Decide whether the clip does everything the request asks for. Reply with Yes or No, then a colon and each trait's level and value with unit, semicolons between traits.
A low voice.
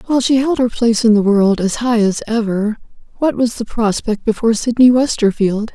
No: high, 225 Hz